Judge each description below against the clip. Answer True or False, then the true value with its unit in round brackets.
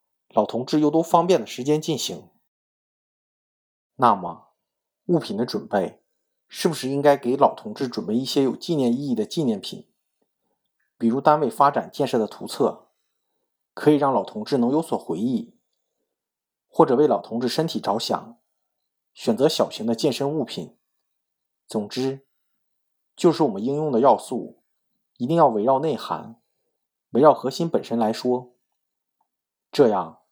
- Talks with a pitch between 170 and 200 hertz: False (140 Hz)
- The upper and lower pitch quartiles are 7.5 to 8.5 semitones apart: False (5.6 semitones)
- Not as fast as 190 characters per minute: False (220 characters per minute)